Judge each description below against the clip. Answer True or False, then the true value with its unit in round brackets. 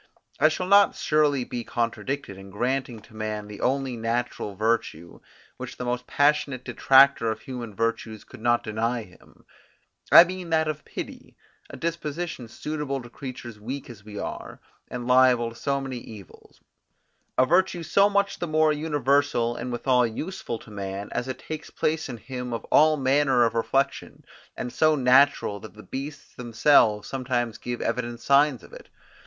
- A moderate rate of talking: True (170 wpm)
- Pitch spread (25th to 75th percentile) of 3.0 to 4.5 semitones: True (4.0 semitones)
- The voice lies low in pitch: True (125 Hz)